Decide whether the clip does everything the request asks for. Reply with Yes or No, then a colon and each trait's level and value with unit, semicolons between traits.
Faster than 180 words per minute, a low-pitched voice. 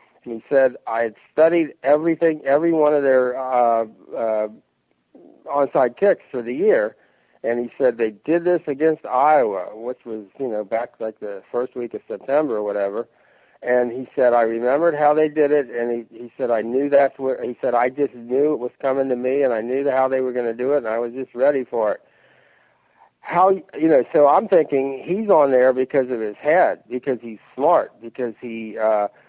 Yes: fast, 205 wpm; low, 130 Hz